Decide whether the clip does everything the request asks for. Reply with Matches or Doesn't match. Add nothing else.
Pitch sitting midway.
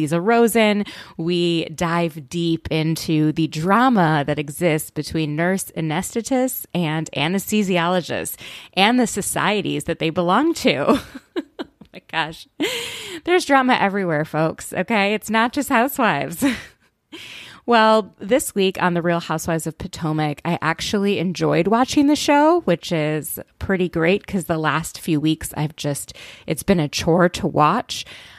Matches